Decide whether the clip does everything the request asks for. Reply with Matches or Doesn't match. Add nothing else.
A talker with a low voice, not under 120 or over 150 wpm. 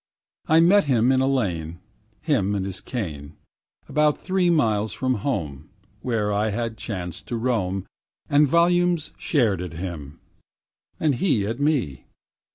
Matches